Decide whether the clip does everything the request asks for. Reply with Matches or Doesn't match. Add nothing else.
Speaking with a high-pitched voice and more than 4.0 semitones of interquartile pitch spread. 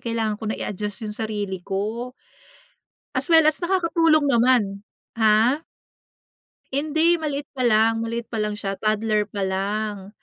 Matches